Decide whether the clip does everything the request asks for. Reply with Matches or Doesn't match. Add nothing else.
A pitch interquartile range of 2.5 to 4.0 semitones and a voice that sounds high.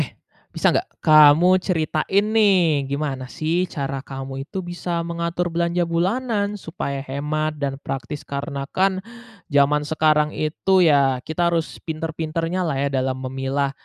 Doesn't match